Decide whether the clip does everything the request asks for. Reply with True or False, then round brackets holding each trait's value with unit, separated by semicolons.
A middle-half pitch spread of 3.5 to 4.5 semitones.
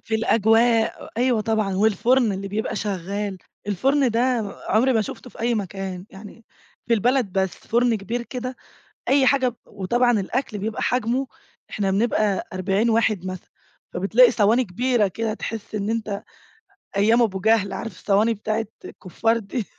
False (3.1 semitones)